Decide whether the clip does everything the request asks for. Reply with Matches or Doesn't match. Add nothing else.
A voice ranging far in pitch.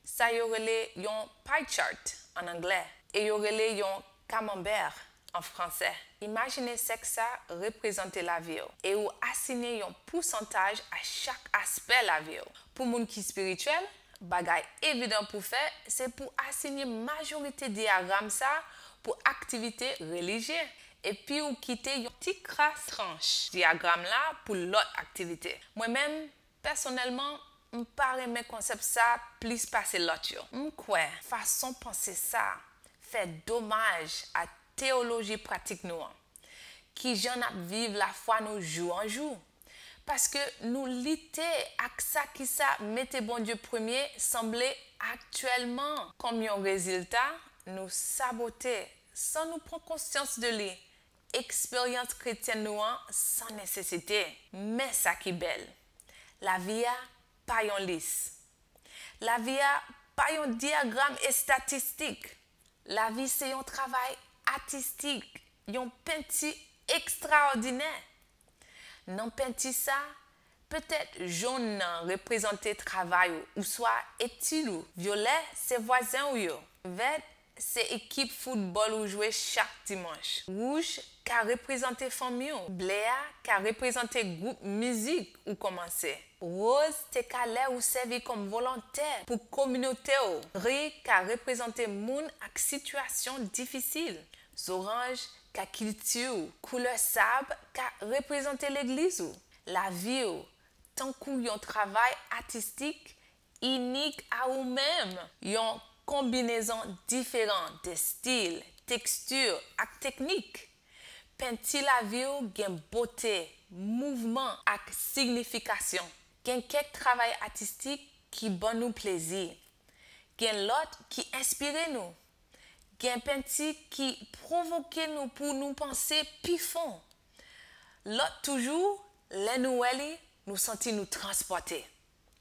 Doesn't match